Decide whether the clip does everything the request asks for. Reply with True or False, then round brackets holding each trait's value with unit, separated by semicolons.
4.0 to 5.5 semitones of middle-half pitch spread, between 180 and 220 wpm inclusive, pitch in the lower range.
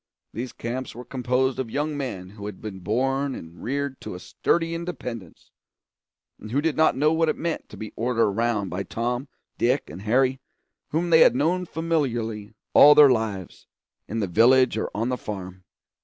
True (4.8 semitones; 185 wpm; 125 Hz)